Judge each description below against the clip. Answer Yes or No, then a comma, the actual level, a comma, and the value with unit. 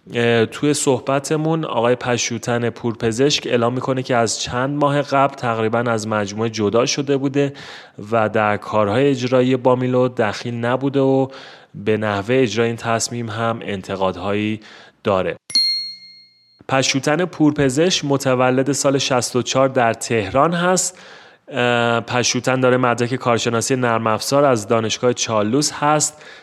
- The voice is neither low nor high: No, low, 125 Hz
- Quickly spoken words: No, average, 115 wpm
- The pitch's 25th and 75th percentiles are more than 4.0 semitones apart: No, average, 3.2 semitones